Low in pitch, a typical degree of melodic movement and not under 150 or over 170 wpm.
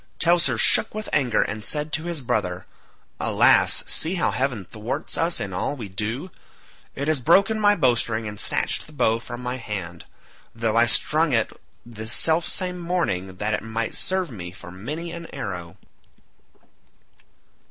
No: low, 120 Hz; wide, 7.4 semitones; average, 165 wpm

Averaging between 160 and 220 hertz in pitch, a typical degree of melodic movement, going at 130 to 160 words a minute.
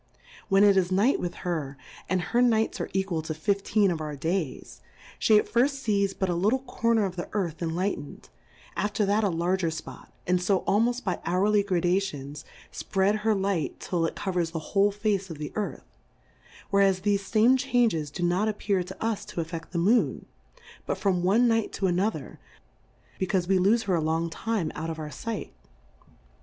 No: high, 190 Hz; average, 3.5 semitones; average, 190 wpm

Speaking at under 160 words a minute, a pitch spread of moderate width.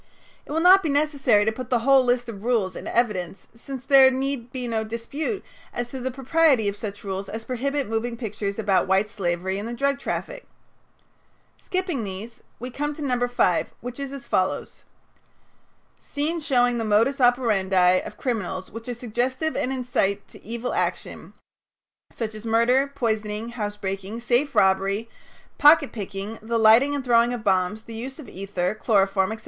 No: average, 175 wpm; average, 4.2 semitones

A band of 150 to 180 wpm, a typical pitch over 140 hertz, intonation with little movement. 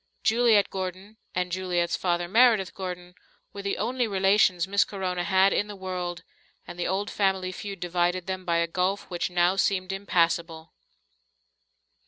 Yes: average, 155 wpm; medium, 185 Hz; narrow, 1.9 semitones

